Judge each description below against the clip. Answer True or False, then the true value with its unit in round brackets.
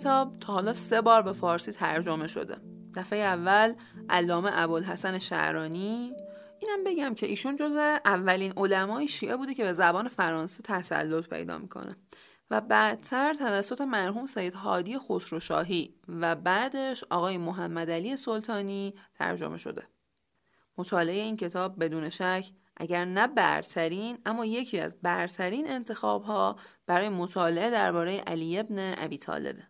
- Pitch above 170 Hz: True (190 Hz)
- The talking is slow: True (130 wpm)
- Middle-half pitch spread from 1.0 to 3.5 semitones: False (4.6 semitones)